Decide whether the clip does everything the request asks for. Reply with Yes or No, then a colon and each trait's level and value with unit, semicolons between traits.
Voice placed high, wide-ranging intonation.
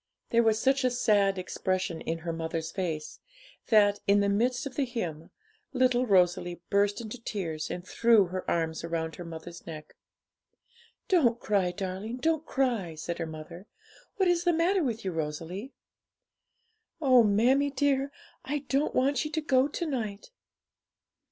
Yes: high, 205 Hz; wide, 7.0 semitones